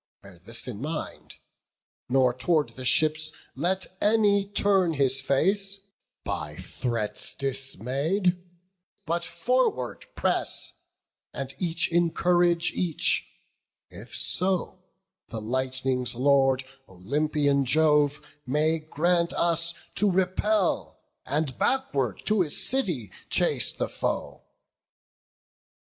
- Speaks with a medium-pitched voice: Yes, medium, 155 Hz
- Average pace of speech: No, slow, 100 wpm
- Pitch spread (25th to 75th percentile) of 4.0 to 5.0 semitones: No, wide, 5.4 semitones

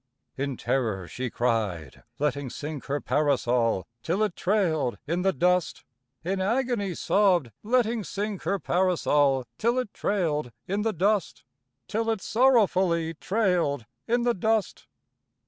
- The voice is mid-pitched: Yes, medium, 180 Hz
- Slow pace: Yes, slow, 130 wpm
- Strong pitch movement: Yes, wide, 6.9 semitones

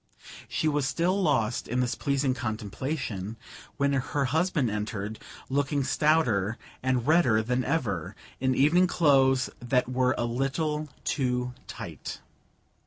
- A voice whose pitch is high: No, low, 130 Hz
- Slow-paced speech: Yes, slow, 125 wpm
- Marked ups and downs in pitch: No, average, 3.7 semitones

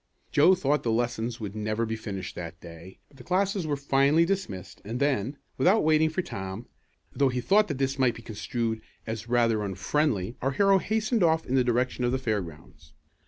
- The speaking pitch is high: No, low, 125 Hz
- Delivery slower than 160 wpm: No, average, 185 wpm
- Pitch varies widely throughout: Yes, wide, 6.0 semitones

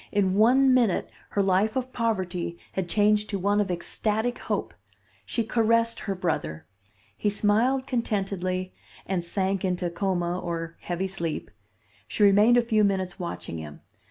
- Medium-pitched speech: No, high, 195 Hz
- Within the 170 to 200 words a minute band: No, average, 150 wpm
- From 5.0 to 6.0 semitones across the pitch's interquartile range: No, average, 3.5 semitones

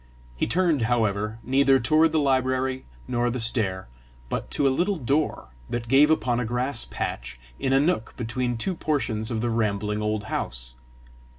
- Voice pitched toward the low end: Yes, low, 120 Hz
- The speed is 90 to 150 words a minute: No, average, 170 wpm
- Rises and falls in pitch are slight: No, average, 3.9 semitones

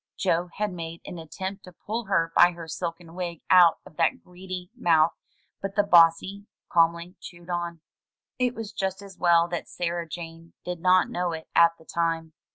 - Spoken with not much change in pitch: Yes, narrow, 1.8 semitones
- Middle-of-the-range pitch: Yes, medium, 175 Hz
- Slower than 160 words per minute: No, average, 180 wpm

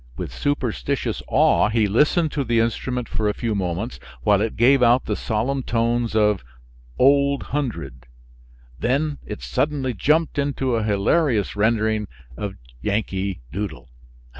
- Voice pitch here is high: No, low, 115 Hz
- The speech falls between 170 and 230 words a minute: No, average, 140 wpm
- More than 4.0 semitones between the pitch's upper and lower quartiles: Yes, average, 4.5 semitones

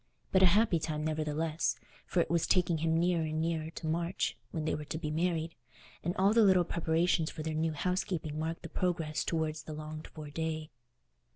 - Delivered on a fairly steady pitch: Yes, narrow, 1.8 semitones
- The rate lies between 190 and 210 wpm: Yes, average, 200 wpm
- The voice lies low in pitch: No, medium, 160 Hz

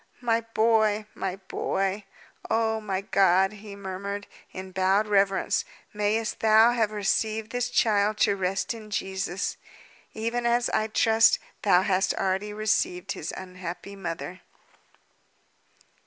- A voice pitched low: No, high, 205 Hz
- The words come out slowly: Yes, slow, 125 wpm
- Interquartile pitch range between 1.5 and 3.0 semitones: Yes, narrow, 2.4 semitones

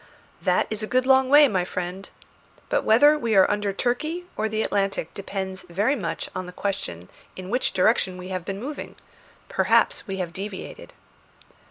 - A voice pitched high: Yes, high, 200 Hz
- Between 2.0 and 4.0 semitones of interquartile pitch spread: No, average, 4.5 semitones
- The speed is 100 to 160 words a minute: No, average, 175 wpm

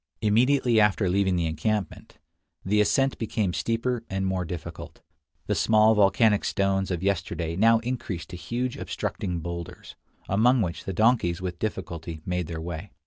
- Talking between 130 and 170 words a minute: Yes, average, 150 wpm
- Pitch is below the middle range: Yes, very low, 95 Hz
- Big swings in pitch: No, average, 4.1 semitones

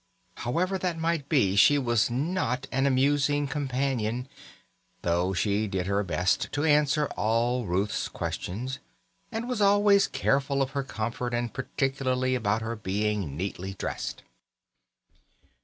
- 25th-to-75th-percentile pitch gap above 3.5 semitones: Yes, wide, 5.4 semitones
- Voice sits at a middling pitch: No, low, 125 Hz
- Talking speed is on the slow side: Yes, slow, 130 wpm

